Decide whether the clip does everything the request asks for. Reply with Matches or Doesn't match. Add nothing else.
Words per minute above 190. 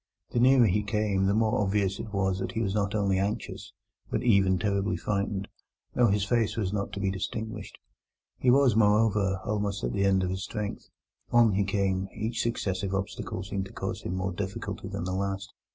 Matches